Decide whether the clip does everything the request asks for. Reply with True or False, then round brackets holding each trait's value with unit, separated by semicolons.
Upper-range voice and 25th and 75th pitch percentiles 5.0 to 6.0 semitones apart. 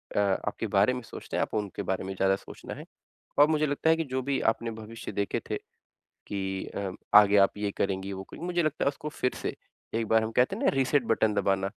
False (110 Hz; 5.4 semitones)